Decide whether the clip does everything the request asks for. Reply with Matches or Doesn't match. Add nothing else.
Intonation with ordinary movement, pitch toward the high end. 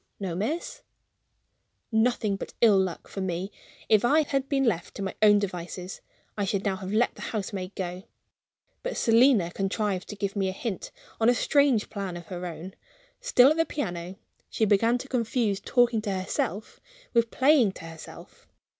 Matches